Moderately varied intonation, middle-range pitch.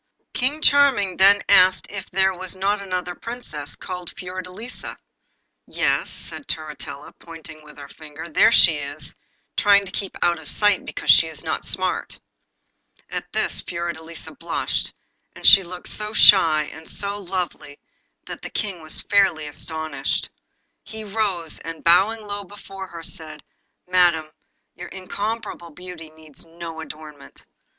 Yes: average, 4.0 semitones; medium, 180 Hz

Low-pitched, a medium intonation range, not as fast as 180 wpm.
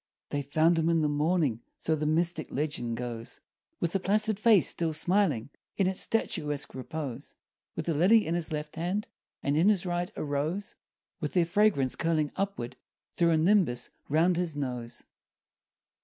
No: medium, 160 Hz; average, 3.8 semitones; average, 170 wpm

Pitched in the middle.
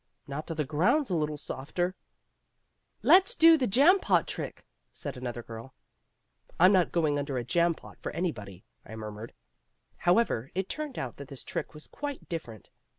Yes: medium, 155 Hz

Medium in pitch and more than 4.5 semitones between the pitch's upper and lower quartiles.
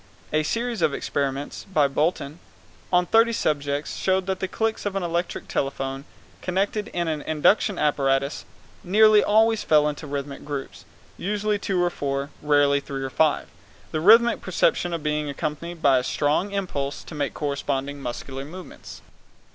Yes: medium, 155 Hz; average, 5.2 semitones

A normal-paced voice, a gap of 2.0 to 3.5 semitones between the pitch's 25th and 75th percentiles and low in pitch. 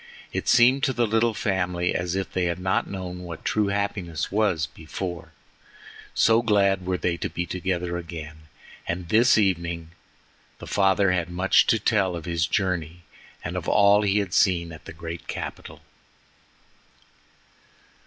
Yes: average, 155 wpm; average, 2.8 semitones; very low, 90 Hz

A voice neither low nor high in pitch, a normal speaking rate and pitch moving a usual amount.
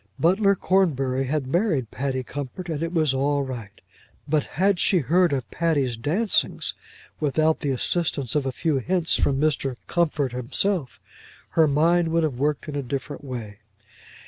Yes: medium, 145 Hz; average, 160 wpm; average, 4.1 semitones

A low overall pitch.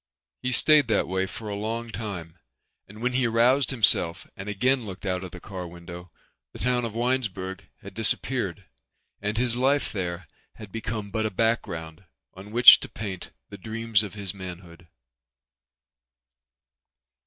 Yes: low, 105 Hz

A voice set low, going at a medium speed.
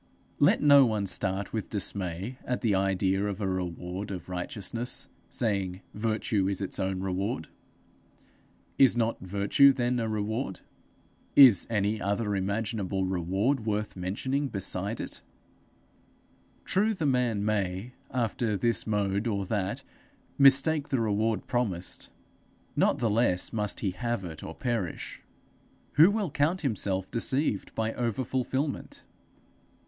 No: low, 105 Hz; slow, 130 wpm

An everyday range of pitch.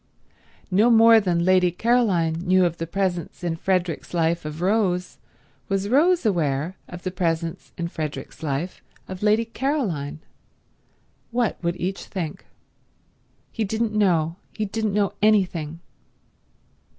Yes: average, 4.1 semitones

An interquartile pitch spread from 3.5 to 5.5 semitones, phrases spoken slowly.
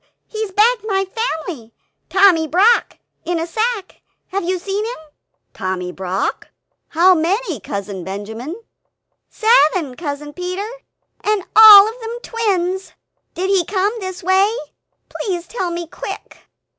Yes: average, 4.9 semitones; slow, 130 wpm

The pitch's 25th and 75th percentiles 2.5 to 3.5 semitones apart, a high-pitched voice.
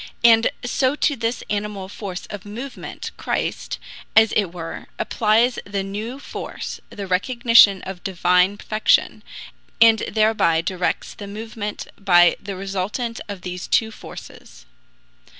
Yes: average, 3.1 semitones; high, 205 Hz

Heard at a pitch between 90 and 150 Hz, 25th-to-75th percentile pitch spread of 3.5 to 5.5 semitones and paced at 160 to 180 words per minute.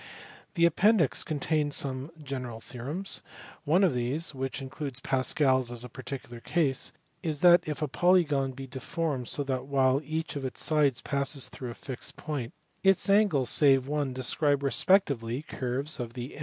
No: medium, 140 Hz; average, 3.1 semitones; average, 165 wpm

